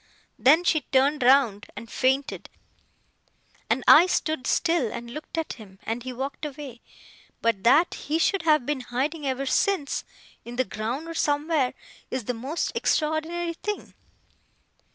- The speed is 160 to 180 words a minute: No, average, 150 wpm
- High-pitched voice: Yes, very high, 280 Hz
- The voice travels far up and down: No, average, 4.3 semitones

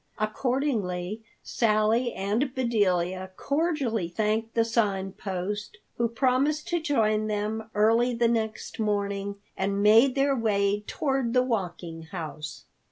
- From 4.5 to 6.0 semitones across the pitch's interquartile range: No, average, 3.3 semitones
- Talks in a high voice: Yes, high, 215 Hz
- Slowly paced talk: Yes, slow, 120 wpm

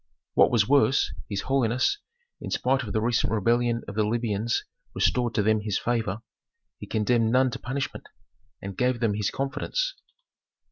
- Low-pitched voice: Yes, low, 115 Hz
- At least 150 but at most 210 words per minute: Yes, average, 160 wpm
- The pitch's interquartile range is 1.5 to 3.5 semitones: Yes, average, 2.8 semitones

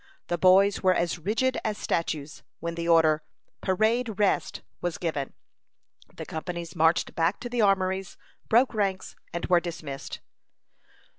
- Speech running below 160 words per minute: Yes, average, 140 wpm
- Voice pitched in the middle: Yes, medium, 180 Hz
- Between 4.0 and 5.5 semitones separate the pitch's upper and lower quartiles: No, average, 3.5 semitones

